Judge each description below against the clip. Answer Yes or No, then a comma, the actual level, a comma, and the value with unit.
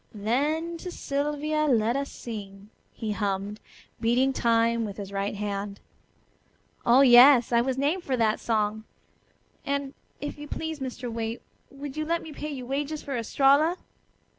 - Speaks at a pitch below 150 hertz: No, very high, 250 Hz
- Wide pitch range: No, average, 4.8 semitones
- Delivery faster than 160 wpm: No, average, 155 wpm